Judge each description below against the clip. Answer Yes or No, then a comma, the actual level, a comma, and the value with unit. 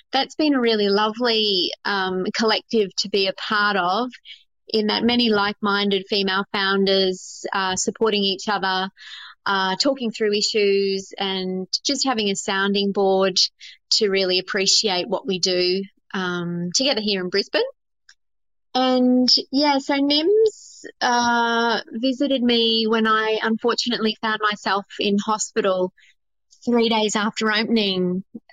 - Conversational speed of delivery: No, slow, 130 wpm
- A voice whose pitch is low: No, high, 210 Hz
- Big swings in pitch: No, average, 3.3 semitones